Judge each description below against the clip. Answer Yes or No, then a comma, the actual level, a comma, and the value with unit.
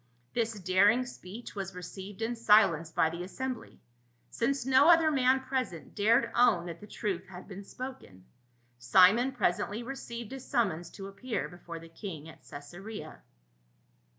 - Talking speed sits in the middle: Yes, average, 150 wpm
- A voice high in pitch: Yes, high, 205 Hz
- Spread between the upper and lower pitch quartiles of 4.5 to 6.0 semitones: Yes, wide, 5.6 semitones